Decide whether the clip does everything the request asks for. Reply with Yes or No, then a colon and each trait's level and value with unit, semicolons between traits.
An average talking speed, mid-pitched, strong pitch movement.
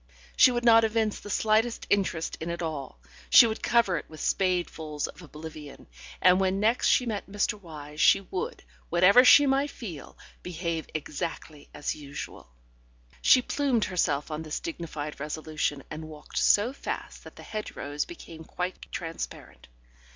Yes: average, 160 wpm; medium, 175 Hz; wide, 5.9 semitones